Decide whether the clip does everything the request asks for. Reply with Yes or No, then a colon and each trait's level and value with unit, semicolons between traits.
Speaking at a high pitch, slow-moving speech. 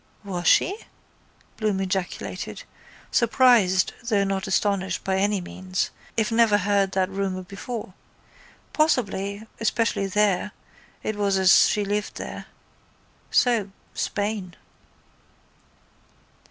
Yes: high, 200 Hz; slow, 100 wpm